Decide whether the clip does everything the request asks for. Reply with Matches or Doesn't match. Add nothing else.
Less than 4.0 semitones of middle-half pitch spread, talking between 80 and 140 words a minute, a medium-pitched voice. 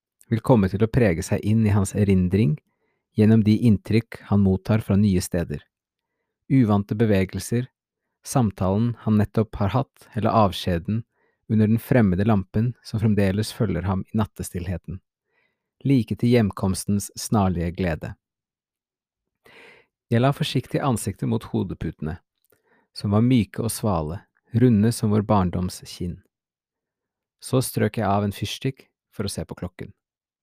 Doesn't match